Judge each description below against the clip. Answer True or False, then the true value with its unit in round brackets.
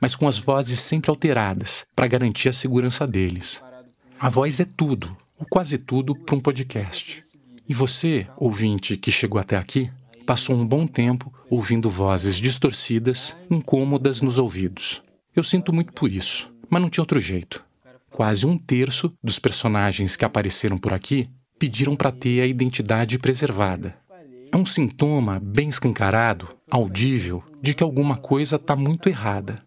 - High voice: False (130 Hz)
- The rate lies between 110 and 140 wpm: False (155 wpm)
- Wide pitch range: False (4.4 semitones)